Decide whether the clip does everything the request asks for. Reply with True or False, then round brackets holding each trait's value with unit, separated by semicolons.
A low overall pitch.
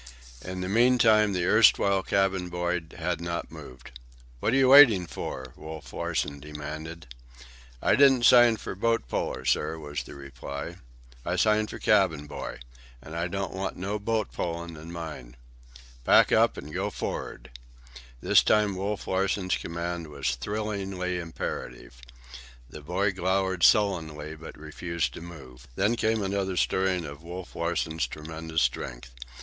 True (85 Hz)